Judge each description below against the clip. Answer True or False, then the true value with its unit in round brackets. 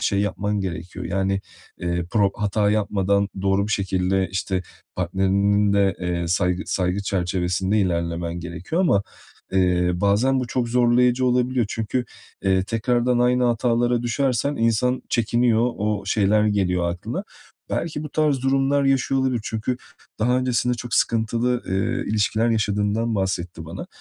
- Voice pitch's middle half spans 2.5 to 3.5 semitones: False (4.3 semitones)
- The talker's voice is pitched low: True (105 Hz)